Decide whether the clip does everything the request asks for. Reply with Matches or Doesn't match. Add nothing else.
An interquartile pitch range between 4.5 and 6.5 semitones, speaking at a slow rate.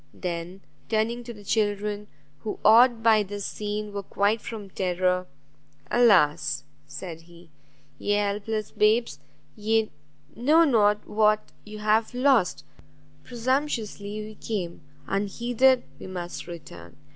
Doesn't match